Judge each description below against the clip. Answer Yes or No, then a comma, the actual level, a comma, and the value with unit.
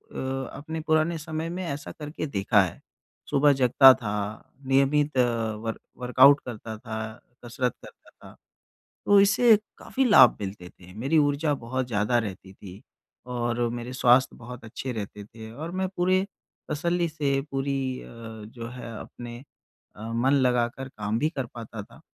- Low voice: Yes, low, 125 Hz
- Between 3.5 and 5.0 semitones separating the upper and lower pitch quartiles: Yes, average, 4.5 semitones